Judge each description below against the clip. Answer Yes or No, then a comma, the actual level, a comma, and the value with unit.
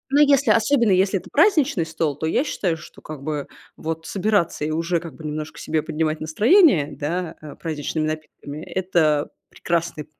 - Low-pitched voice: No, medium, 160 Hz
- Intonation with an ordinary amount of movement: Yes, average, 3.9 semitones